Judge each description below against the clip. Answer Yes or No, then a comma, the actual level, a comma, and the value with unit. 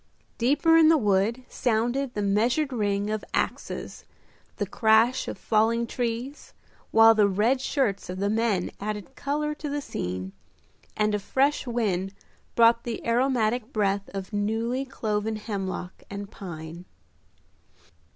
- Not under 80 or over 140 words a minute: Yes, slow, 135 wpm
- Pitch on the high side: Yes, high, 220 Hz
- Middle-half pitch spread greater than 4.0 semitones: No, average, 3.7 semitones